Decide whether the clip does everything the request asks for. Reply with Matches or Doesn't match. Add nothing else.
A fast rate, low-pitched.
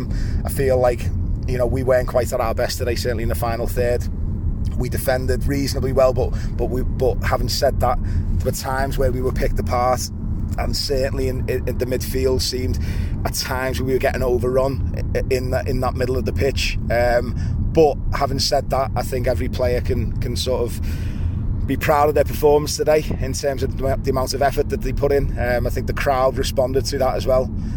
Matches